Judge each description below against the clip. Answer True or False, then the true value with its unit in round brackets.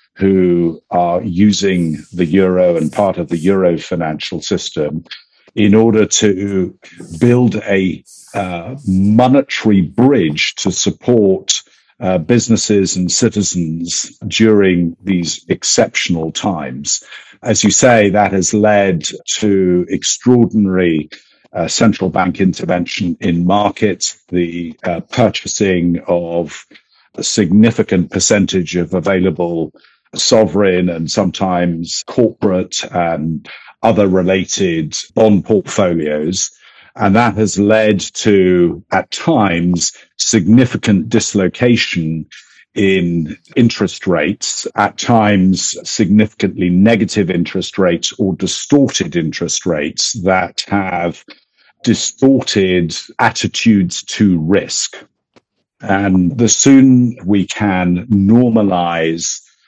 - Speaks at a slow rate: True (95 wpm)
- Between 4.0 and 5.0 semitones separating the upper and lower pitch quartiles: False (3.6 semitones)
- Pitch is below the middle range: True (95 Hz)